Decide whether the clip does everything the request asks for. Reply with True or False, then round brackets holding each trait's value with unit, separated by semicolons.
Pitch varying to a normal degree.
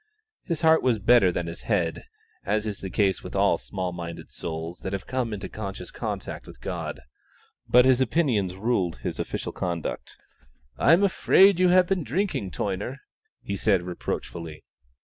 False (6.3 semitones)